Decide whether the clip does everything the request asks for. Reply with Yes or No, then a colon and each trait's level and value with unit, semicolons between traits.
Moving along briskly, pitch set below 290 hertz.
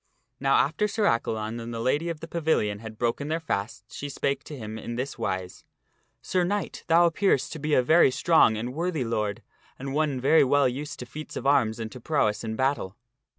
Yes: fast, 215 wpm; low, 135 Hz